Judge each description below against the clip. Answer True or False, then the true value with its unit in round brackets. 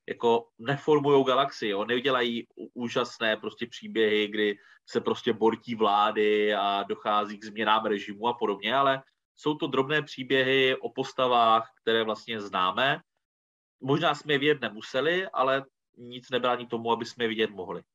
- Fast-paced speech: False (150 wpm)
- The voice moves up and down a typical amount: True (3.6 semitones)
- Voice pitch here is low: True (115 Hz)